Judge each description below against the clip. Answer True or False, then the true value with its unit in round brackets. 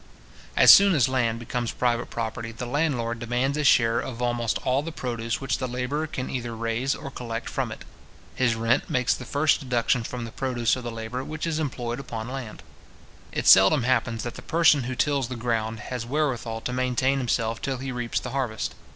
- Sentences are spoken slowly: False (205 wpm)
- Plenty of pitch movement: False (2.5 semitones)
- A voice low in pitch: True (125 Hz)